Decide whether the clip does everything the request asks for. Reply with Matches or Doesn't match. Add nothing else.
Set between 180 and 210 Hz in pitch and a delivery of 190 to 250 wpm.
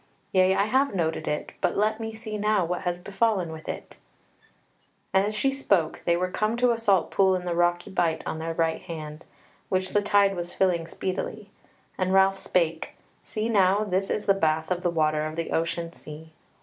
Matches